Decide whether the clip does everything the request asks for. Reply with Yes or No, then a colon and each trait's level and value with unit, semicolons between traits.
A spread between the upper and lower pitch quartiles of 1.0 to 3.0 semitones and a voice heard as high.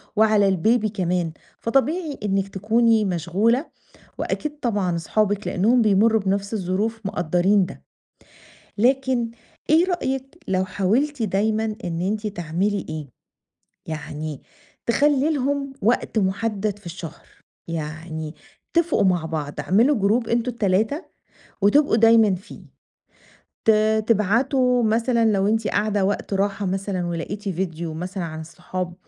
No: average, 4.1 semitones; high, 205 Hz